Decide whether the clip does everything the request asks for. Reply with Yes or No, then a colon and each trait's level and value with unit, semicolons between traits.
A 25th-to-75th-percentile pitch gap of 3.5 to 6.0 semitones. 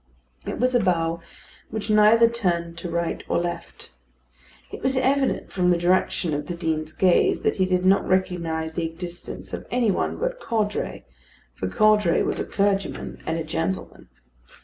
Yes: average, 4.1 semitones